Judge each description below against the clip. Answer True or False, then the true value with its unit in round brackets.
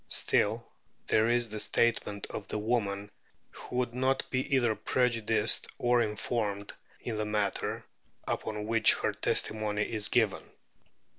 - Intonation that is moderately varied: False (2.3 semitones)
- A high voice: False (110 Hz)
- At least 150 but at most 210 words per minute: False (135 wpm)